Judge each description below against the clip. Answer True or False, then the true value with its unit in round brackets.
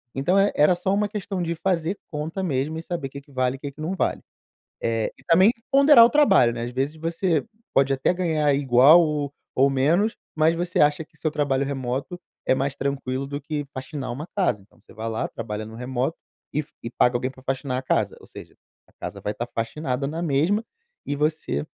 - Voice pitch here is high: False (145 Hz)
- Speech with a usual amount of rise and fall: True (4.2 semitones)